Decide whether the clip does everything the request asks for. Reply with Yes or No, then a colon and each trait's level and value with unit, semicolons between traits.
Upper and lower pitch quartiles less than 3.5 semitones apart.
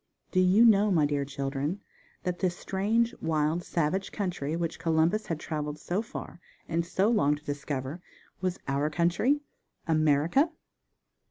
No: average, 4.3 semitones